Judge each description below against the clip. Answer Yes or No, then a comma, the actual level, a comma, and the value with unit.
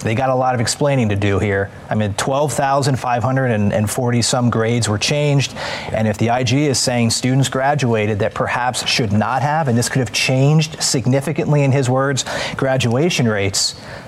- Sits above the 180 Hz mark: No, low, 130 Hz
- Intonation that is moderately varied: Yes, average, 3.6 semitones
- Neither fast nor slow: Yes, average, 170 wpm